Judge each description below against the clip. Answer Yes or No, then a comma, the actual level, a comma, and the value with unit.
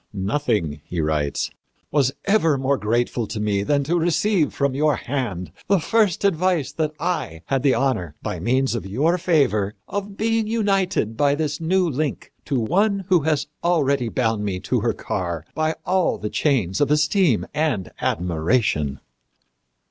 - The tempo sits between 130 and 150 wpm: No, average, 160 wpm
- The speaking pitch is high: No, medium, 140 Hz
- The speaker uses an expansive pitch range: Yes, wide, 8.1 semitones